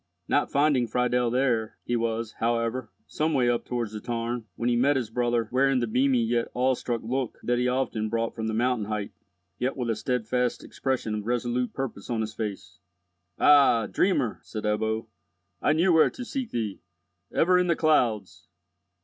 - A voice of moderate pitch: No, low, 120 Hz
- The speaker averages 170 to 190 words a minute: Yes, average, 180 wpm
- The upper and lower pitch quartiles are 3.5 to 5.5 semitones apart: No, average, 2.7 semitones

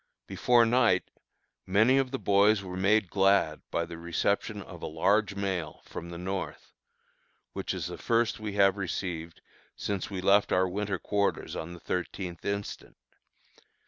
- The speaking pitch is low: Yes, low, 100 Hz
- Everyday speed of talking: Yes, average, 155 wpm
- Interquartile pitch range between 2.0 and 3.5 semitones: Yes, average, 2.7 semitones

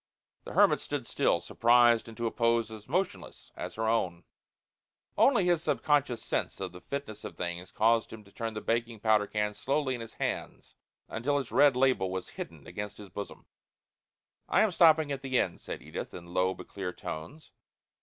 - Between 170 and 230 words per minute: Yes, average, 185 wpm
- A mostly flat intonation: No, average, 4.7 semitones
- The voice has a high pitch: No, low, 115 Hz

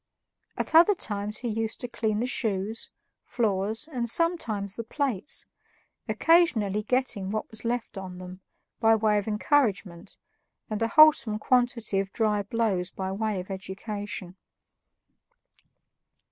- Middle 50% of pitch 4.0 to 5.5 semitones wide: No, average, 3.1 semitones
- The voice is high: Yes, high, 215 Hz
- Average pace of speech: No, slow, 130 wpm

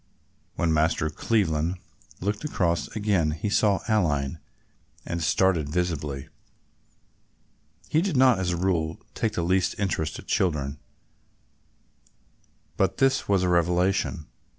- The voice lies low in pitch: Yes, very low, 90 Hz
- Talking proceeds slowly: Yes, slow, 120 wpm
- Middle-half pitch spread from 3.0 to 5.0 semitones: Yes, average, 4.1 semitones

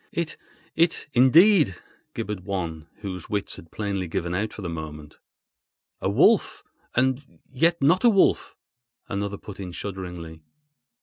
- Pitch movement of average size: No, wide, 7.4 semitones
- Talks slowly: Yes, slow, 120 wpm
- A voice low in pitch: Yes, low, 100 Hz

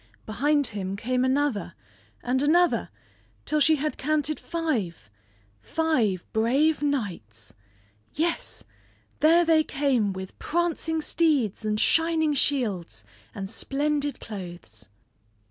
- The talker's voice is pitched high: Yes, very high, 275 Hz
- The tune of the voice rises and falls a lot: Yes, wide, 7.2 semitones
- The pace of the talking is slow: Yes, slow, 105 wpm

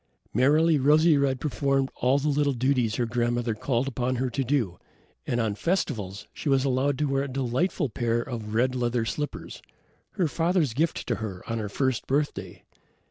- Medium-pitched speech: No, low, 130 Hz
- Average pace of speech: Yes, average, 180 wpm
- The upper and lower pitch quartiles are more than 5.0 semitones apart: No, average, 3.4 semitones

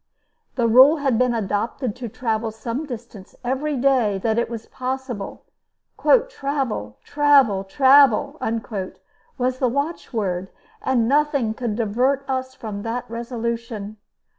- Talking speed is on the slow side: Yes, slow, 120 wpm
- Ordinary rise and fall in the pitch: Yes, average, 3.5 semitones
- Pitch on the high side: Yes, high, 240 Hz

